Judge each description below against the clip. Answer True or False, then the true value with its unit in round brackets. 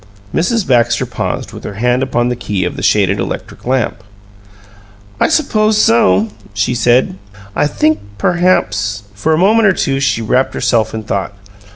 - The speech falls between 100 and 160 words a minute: False (170 wpm)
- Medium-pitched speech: False (120 Hz)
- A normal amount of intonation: False (7.0 semitones)